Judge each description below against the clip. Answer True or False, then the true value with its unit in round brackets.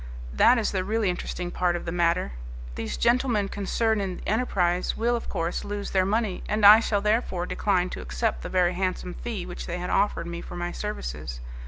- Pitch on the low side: False (185 Hz)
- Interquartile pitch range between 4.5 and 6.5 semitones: False (3.3 semitones)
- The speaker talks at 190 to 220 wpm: True (205 wpm)